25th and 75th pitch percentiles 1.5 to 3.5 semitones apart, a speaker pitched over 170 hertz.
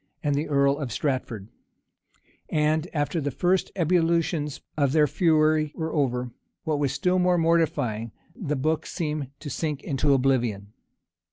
No: average, 2.9 semitones; medium, 150 Hz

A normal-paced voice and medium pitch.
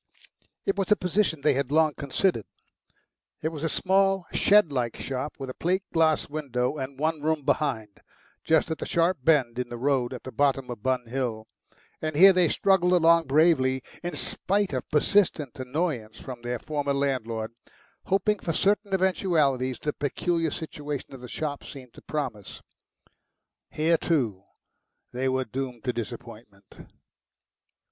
Yes: average, 155 wpm; medium, 145 Hz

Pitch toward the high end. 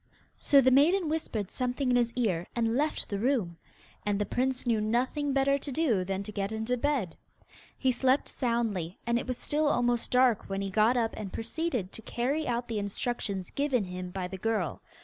Yes: high, 235 Hz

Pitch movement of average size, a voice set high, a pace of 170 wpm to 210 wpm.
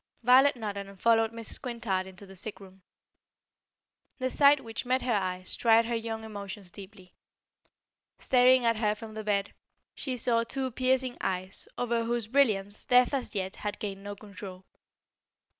No: average, 3.7 semitones; high, 220 Hz; average, 160 wpm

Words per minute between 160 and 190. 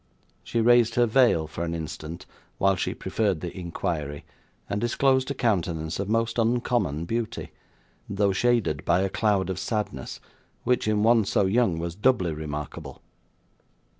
No: average, 150 wpm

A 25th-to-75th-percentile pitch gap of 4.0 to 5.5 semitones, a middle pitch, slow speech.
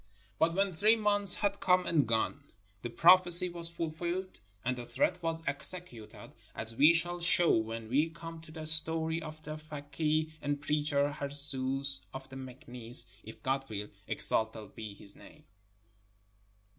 No: average, 4.5 semitones; medium, 155 Hz; average, 155 wpm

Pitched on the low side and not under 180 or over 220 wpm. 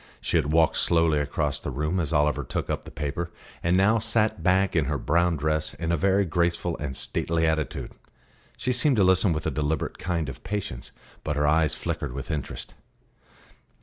Yes: very low, 80 Hz; average, 190 wpm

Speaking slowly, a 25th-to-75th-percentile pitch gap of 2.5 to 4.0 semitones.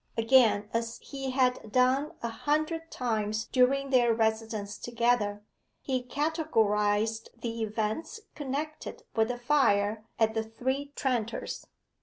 Yes: slow, 120 wpm; average, 3.5 semitones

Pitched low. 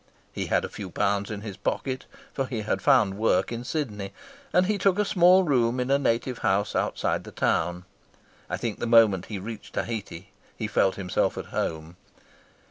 Yes: low, 115 Hz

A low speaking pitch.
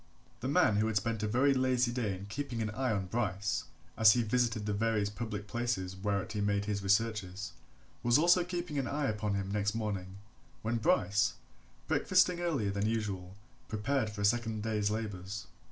Yes: low, 105 Hz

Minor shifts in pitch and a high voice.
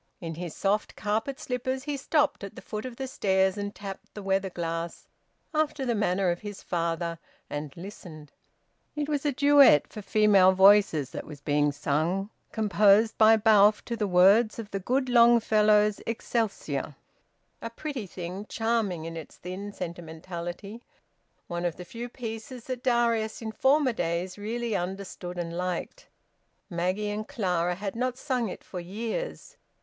No: average, 4.7 semitones; high, 205 Hz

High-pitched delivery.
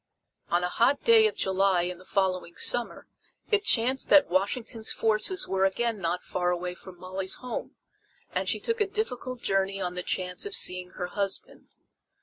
Yes: high, 195 Hz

